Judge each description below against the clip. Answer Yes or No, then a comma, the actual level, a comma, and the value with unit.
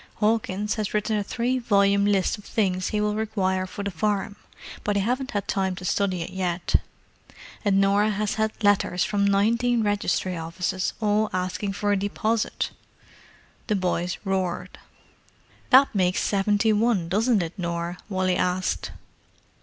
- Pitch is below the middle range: No, high, 200 Hz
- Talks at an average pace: Yes, average, 155 wpm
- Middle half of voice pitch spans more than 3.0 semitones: No, narrow, 2.4 semitones